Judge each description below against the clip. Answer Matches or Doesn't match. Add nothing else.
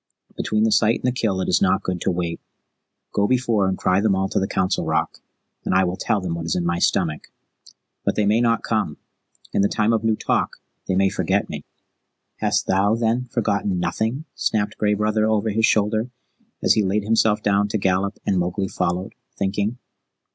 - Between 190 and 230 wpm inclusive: Matches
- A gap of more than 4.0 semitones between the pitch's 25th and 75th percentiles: Doesn't match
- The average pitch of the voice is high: Doesn't match